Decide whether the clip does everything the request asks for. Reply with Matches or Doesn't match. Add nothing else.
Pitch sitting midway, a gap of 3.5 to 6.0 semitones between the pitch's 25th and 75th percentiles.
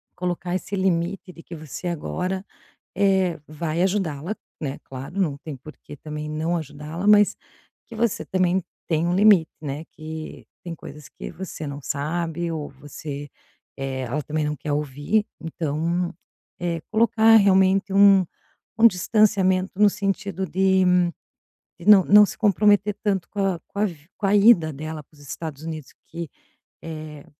Matches